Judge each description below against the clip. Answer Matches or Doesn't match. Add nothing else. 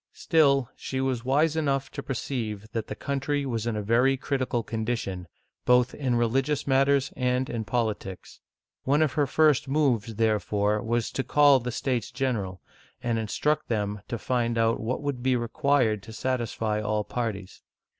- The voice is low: Matches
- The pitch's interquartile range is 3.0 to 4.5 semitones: Matches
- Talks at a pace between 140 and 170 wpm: Matches